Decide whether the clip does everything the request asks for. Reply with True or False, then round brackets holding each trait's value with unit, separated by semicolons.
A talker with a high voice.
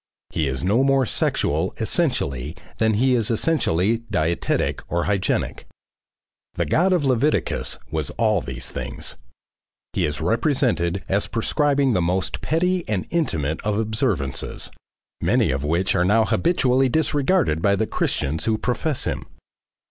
False (110 Hz)